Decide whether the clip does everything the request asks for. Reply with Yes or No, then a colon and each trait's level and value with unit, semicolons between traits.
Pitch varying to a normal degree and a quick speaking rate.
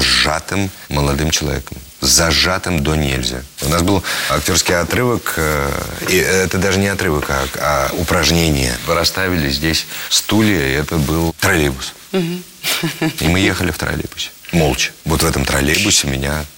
No: average, 4.5 semitones; average, 140 wpm